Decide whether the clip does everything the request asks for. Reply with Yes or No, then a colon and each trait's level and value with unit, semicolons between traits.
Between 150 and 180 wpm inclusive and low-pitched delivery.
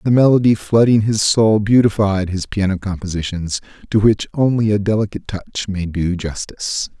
Yes: average, 155 wpm; low, 100 Hz